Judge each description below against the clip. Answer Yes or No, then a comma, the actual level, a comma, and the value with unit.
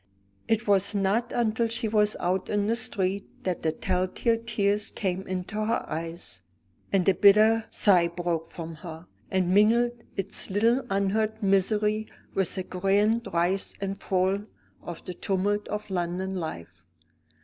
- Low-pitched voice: No, high, 195 Hz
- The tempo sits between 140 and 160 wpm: Yes, average, 150 wpm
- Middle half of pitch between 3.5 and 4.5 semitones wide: No, average, 2.9 semitones